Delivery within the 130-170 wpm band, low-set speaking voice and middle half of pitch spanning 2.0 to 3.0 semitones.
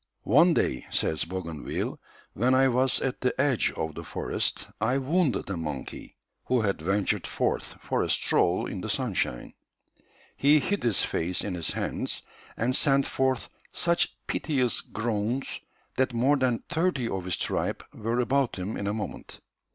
No: average, 160 wpm; low, 120 Hz; wide, 5.5 semitones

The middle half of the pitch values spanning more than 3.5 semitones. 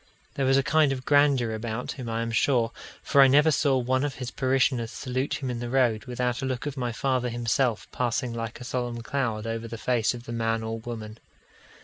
No: narrow, 2.4 semitones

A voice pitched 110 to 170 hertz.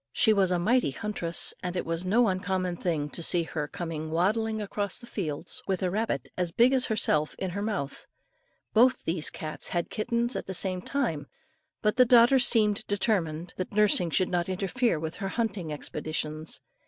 No: medium, 185 Hz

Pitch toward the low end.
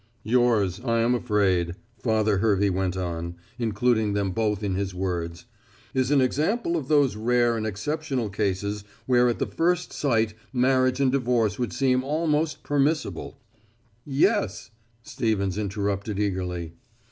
Yes: low, 110 Hz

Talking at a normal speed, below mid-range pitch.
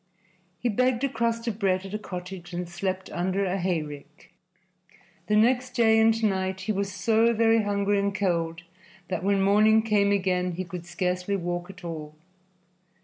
No: average, 170 wpm; high, 195 Hz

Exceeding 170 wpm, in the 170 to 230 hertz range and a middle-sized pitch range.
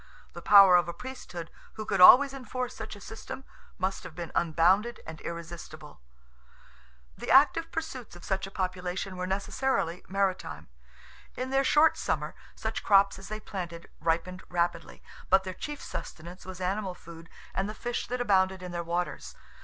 No: average, 165 wpm; high, 190 Hz; average, 4.0 semitones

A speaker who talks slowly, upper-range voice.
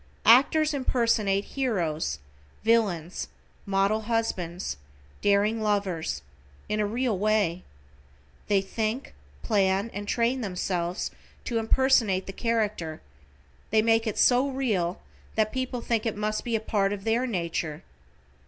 Yes: slow, 125 wpm; high, 215 Hz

